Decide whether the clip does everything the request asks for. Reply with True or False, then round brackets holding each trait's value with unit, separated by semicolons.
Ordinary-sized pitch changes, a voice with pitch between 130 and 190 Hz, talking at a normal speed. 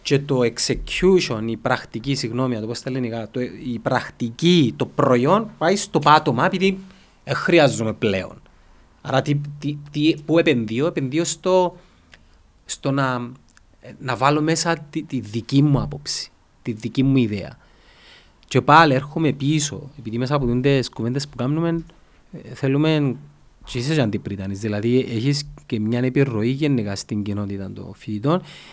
True (4.5 semitones; 135 Hz; 140 wpm)